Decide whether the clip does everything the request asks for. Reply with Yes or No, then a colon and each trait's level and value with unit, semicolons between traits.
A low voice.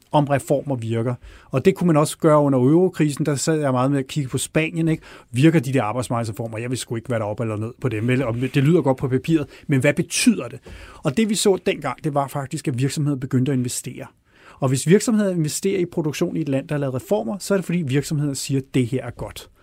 No: medium, 145 Hz